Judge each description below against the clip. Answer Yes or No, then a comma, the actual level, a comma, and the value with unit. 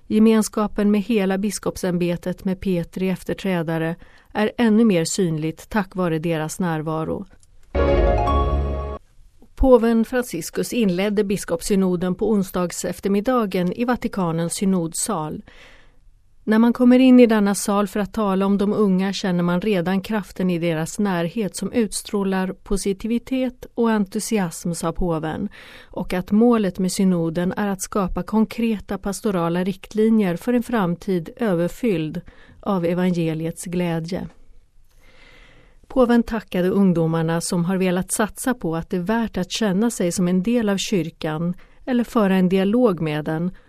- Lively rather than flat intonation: No, average, 3.9 semitones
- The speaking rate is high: No, average, 130 wpm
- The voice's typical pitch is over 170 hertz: Yes, high, 190 Hz